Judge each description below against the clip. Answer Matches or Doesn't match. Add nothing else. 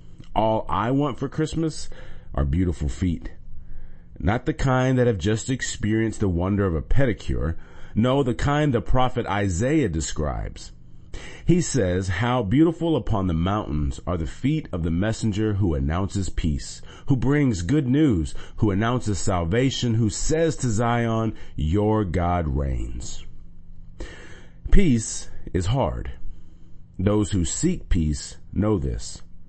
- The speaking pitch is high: Doesn't match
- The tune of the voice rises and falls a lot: Matches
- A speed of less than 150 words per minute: Matches